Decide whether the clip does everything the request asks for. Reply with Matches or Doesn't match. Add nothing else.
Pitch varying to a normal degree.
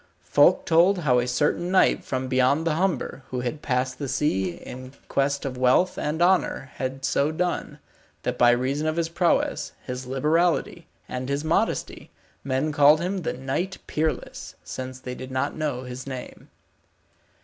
Matches